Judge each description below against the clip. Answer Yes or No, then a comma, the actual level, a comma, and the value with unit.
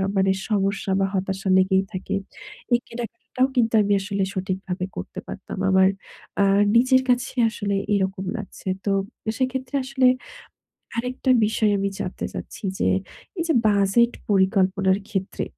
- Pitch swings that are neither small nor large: Yes, average, 3.8 semitones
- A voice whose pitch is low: No, high, 200 Hz